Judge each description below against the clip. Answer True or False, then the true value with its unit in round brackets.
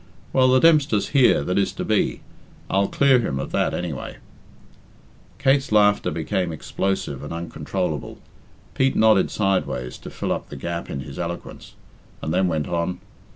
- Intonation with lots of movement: True (5.7 semitones)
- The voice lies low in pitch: True (95 Hz)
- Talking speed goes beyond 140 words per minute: True (155 wpm)